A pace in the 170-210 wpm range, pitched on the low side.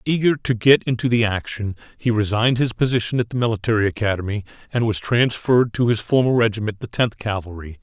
Yes: average, 185 wpm; low, 115 Hz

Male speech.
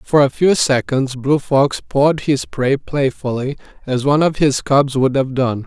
Yes: male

